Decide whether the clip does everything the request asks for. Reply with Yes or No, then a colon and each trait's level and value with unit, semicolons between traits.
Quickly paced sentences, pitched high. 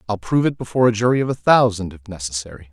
No: fast, 245 wpm; low, 105 Hz